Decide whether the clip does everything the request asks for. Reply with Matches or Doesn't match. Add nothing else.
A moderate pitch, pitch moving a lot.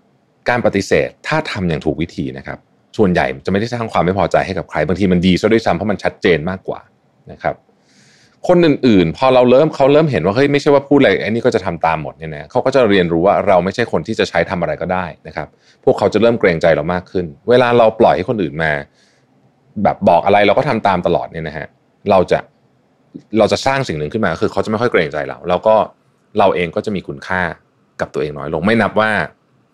Doesn't match